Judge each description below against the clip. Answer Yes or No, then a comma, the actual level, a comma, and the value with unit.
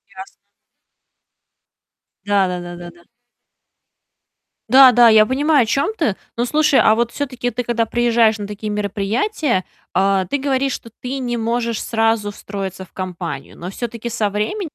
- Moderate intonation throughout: Yes, average, 3.9 semitones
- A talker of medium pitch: No, high, 225 Hz